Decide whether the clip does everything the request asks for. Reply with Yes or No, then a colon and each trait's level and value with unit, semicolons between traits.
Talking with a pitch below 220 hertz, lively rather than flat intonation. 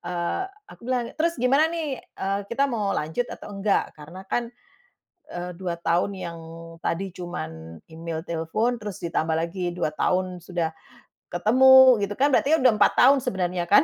Yes: high, 190 Hz; wide, 6.4 semitones